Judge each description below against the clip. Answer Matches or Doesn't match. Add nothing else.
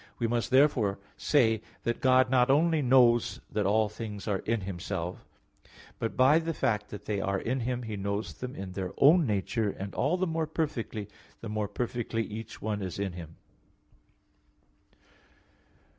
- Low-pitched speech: Matches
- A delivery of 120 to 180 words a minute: Matches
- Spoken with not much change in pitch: Doesn't match